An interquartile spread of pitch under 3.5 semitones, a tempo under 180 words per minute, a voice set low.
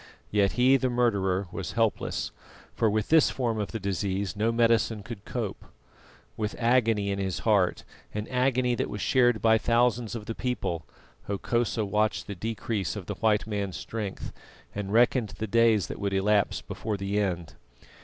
Yes: average, 2.7 semitones; average, 170 wpm; low, 110 Hz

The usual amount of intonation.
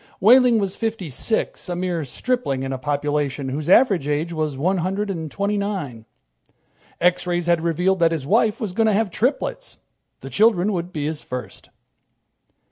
No: wide, 5.7 semitones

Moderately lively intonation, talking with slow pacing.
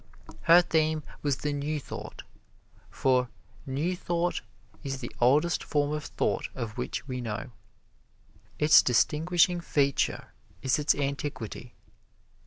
Yes: average, 3.2 semitones; slow, 120 wpm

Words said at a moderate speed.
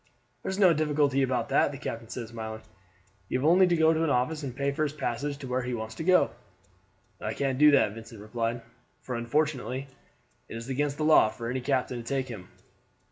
No: fast, 215 wpm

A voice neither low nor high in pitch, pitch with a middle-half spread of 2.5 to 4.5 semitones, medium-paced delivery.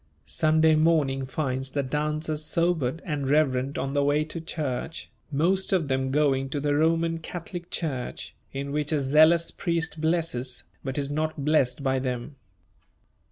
Yes: medium, 150 Hz; average, 3.0 semitones; average, 160 wpm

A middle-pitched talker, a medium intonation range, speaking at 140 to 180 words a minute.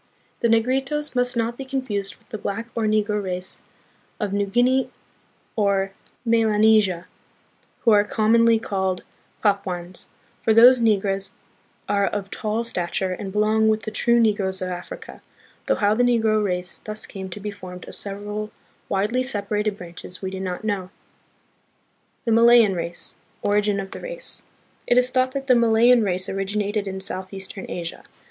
No: high, 210 Hz; average, 3.1 semitones; average, 160 wpm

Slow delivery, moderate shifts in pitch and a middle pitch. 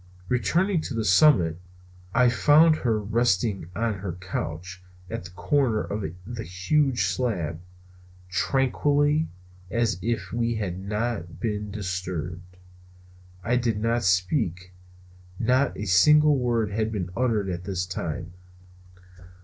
No: slow, 125 wpm; average, 5.0 semitones; low, 105 Hz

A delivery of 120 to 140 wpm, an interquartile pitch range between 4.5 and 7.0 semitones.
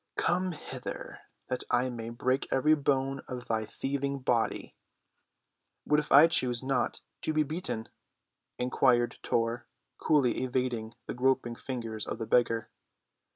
No: slow, 135 wpm; average, 2.7 semitones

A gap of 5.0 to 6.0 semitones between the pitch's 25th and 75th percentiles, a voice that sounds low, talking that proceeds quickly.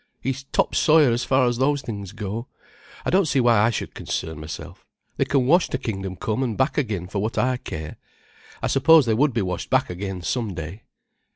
Yes: wide, 5.4 semitones; low, 115 Hz; fast, 210 wpm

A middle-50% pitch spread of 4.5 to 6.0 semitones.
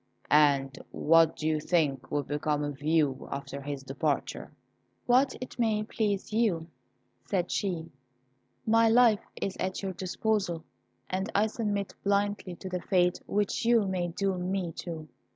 Yes: average, 4.9 semitones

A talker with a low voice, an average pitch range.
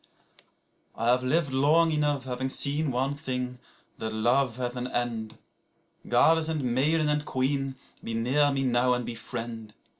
Yes: low, 130 Hz; average, 3.0 semitones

